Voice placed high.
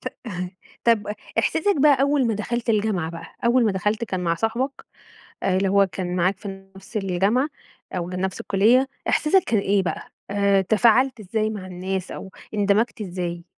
Yes: high, 200 Hz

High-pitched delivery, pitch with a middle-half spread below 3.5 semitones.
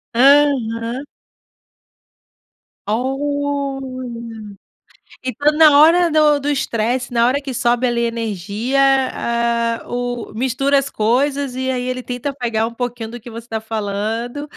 Yes: high, 245 Hz; average, 3.1 semitones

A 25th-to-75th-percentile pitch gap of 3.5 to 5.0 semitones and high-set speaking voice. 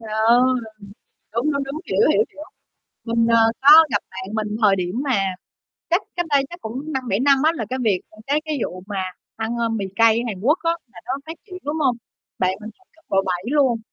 No: wide, 5.5 semitones; high, 235 Hz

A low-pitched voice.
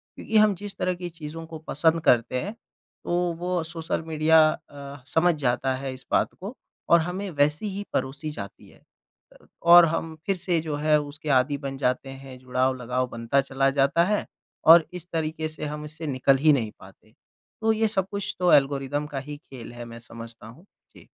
No: medium, 150 Hz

